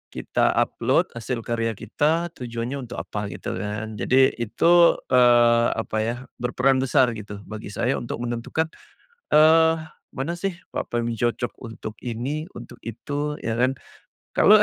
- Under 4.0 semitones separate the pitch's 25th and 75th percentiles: Yes, average, 3.1 semitones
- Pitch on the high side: No, low, 120 Hz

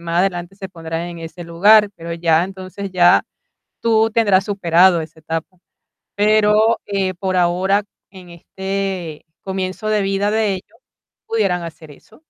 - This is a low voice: No, high, 190 Hz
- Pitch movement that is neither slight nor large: Yes, average, 3.0 semitones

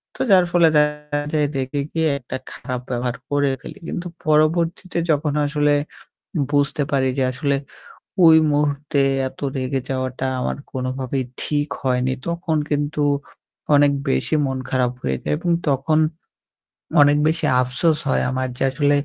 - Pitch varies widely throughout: No, narrow, 2.5 semitones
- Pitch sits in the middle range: Yes, medium, 145 Hz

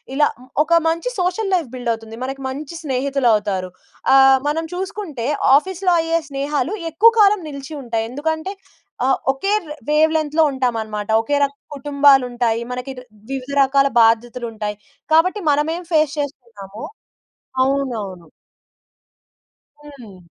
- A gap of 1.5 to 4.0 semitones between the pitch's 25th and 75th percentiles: No, average, 5.0 semitones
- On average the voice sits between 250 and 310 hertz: Yes, very high, 275 Hz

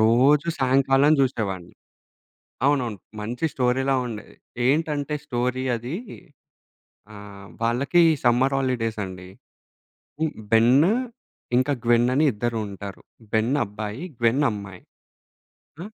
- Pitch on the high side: No, low, 120 Hz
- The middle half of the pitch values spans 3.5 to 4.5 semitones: Yes, average, 3.9 semitones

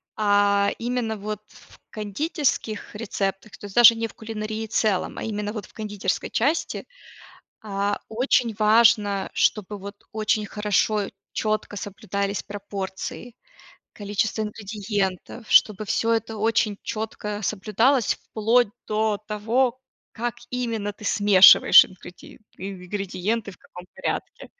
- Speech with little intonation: Yes, narrow, 1.8 semitones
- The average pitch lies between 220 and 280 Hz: No, high, 210 Hz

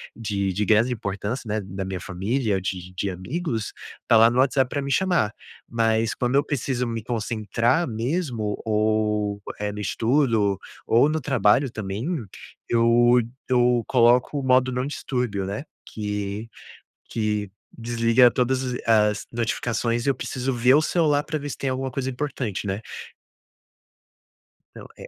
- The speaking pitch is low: Yes, low, 115 Hz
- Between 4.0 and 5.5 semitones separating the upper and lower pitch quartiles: No, average, 3.5 semitones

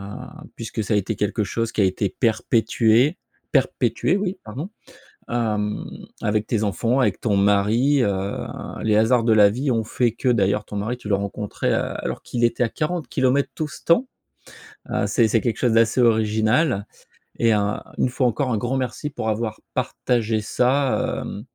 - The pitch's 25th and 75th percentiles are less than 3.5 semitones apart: Yes, average, 3.1 semitones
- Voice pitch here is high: No, low, 115 Hz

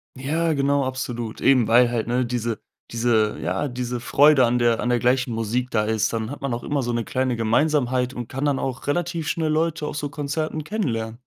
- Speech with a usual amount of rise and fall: Yes, average, 3.5 semitones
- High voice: No, low, 125 Hz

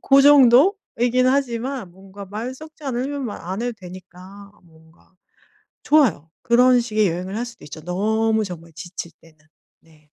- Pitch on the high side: Yes, high, 215 Hz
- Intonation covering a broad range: Yes, wide, 6.0 semitones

